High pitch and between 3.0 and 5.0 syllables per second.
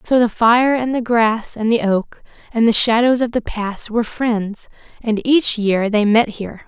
Yes: high, 225 Hz; 4.4 syllables/s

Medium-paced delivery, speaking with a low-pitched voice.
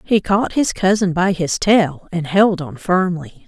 No: average, 190 wpm; medium, 185 Hz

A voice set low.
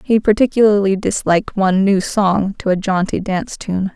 No: high, 195 Hz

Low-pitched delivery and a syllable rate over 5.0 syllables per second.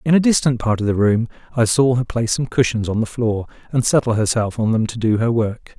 Yes: low, 115 Hz; 5.8 syllables/s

